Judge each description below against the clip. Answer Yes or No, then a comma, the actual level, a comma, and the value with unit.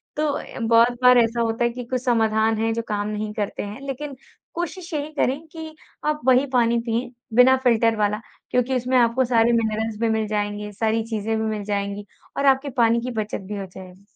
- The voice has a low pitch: No, high, 230 Hz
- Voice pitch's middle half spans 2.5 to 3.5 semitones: Yes, average, 2.8 semitones